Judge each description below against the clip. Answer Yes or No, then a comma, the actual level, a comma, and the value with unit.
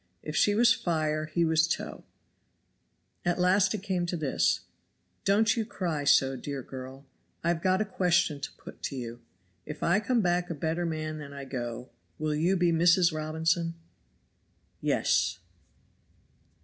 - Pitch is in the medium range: Yes, medium, 165 Hz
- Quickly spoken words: No, average, 160 wpm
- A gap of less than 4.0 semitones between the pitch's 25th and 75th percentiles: Yes, average, 3.6 semitones